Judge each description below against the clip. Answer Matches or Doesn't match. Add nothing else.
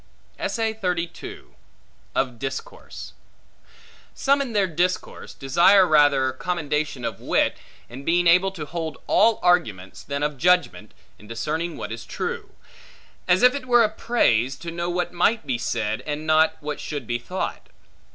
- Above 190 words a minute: Doesn't match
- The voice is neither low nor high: Matches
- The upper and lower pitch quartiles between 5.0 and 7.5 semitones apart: Matches